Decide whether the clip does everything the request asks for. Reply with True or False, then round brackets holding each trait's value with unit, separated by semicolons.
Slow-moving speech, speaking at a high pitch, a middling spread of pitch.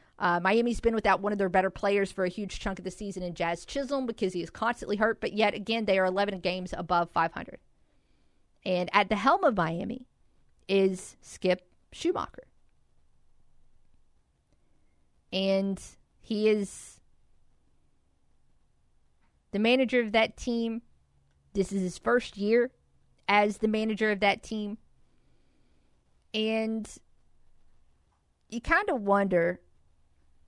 True (130 wpm; 200 Hz; 3.5 semitones)